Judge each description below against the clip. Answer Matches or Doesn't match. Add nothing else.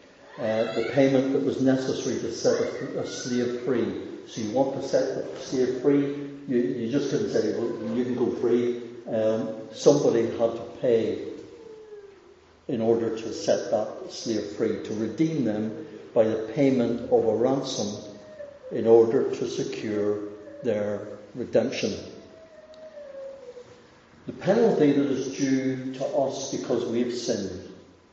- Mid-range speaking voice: Doesn't match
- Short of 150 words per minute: Matches